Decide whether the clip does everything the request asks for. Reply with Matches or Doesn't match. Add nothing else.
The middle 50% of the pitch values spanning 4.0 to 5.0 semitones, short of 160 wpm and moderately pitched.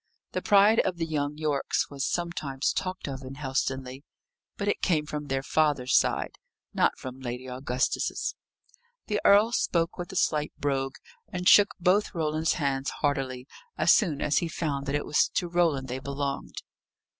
Doesn't match